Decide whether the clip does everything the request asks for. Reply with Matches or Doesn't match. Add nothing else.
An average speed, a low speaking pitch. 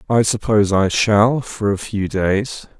Matches